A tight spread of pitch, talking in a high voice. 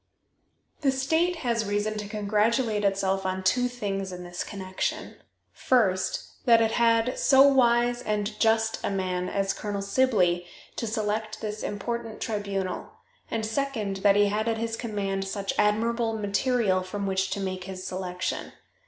No: average, 3.0 semitones; high, 210 Hz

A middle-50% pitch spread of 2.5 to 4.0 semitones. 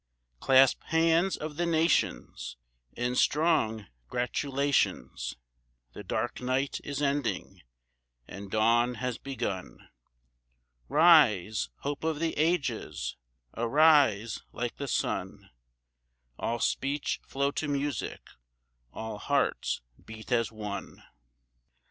No: average, 4.8 semitones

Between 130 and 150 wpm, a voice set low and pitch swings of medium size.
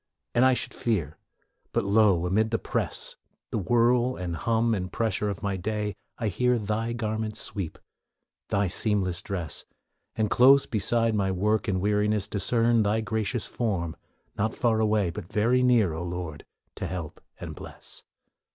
No: average, 160 wpm; low, 105 Hz; average, 3.3 semitones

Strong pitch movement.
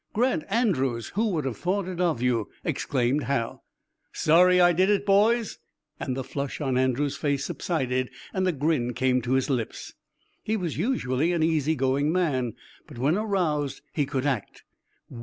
Yes: wide, 5.7 semitones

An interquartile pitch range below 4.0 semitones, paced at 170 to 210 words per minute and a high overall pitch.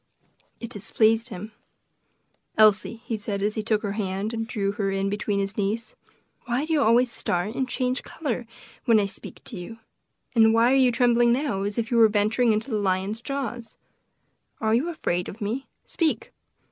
Yes: average, 2.8 semitones; average, 185 wpm; high, 225 Hz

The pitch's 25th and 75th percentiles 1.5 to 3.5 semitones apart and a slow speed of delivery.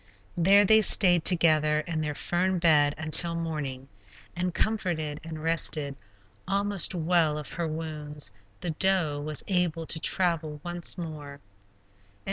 Yes: narrow, 2.6 semitones; slow, 130 wpm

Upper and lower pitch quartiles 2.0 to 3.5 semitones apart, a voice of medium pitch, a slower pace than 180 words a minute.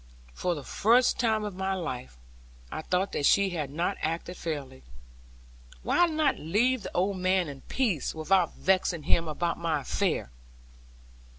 No: average, 4.1 semitones; medium, 180 Hz; average, 155 wpm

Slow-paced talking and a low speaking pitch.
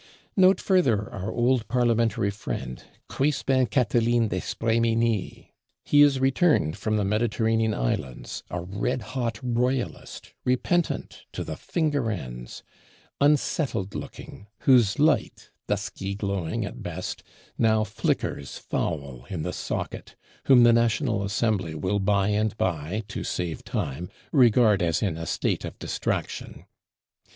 Yes: slow, 125 wpm; low, 110 Hz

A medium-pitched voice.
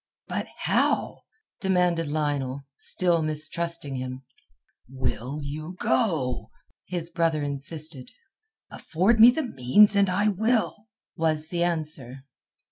Yes: medium, 160 Hz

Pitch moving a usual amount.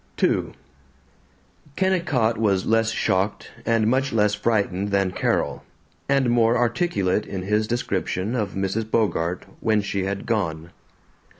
Yes: average, 3.0 semitones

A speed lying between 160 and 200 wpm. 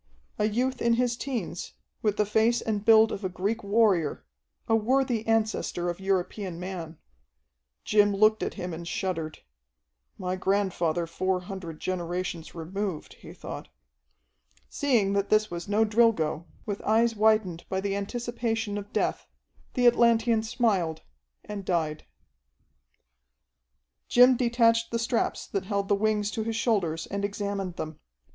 No: average, 140 wpm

